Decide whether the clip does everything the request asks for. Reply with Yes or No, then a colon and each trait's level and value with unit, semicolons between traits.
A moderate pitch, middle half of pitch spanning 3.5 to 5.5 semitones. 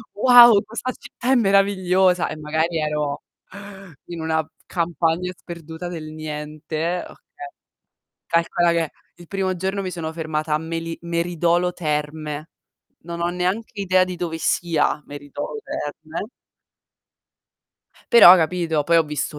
No: medium, 170 Hz; average, 2.7 semitones